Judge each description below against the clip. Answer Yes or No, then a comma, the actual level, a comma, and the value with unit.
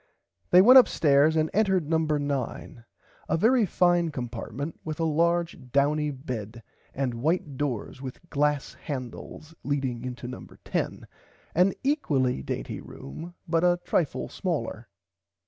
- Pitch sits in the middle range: Yes, medium, 150 Hz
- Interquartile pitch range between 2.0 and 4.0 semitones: No, average, 4.5 semitones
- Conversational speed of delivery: No, slow, 130 wpm